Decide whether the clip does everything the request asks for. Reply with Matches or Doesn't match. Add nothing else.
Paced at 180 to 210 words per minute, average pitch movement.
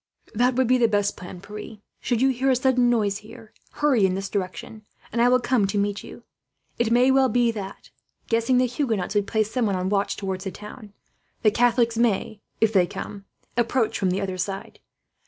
Matches